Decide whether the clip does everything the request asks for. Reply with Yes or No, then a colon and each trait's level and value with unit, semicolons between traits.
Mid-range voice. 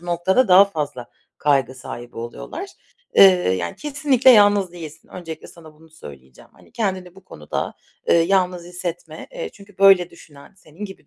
Yes: medium, 175 Hz